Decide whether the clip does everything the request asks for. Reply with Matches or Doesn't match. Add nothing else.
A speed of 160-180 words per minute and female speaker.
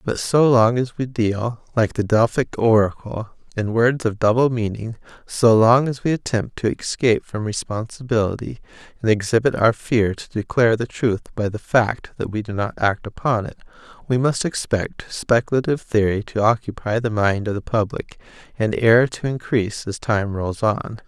Doesn't match